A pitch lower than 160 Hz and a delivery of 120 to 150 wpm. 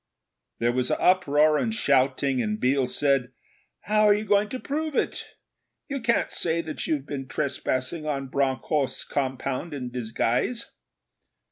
Yes: medium, 140 Hz; average, 140 wpm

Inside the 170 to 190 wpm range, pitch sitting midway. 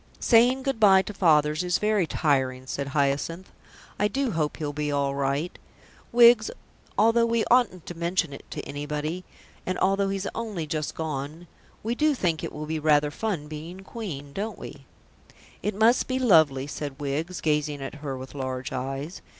Yes: average, 175 wpm; medium, 160 Hz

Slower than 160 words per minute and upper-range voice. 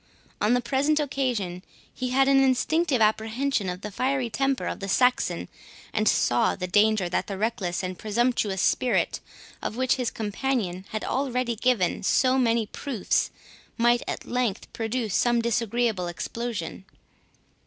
Yes: average, 145 wpm; high, 235 Hz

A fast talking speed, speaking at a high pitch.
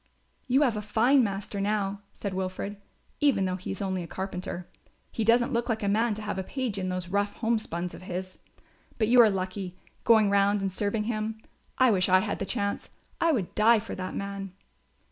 Yes: fast, 210 wpm; high, 200 Hz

